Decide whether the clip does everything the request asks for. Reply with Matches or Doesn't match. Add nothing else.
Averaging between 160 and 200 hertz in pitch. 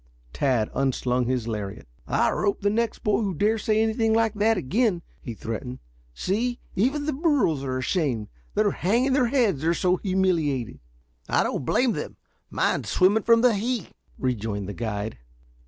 Matches